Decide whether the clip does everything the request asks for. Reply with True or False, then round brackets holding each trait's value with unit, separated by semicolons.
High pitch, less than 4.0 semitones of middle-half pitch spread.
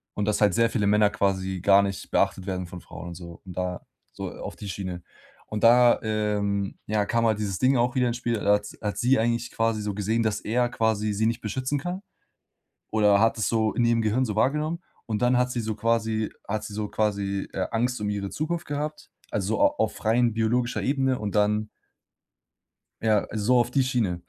False (110 Hz; 2.8 semitones)